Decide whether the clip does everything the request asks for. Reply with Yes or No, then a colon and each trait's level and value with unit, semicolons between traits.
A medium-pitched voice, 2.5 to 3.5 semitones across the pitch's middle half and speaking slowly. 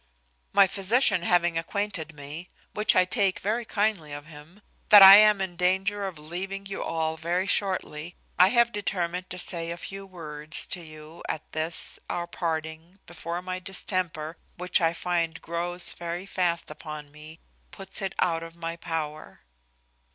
No: medium, 175 Hz; average, 3.1 semitones; average, 160 wpm